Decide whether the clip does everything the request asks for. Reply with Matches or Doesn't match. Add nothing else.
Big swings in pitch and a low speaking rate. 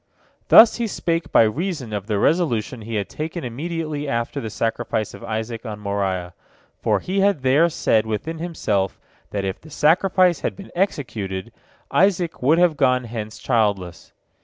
Doesn't match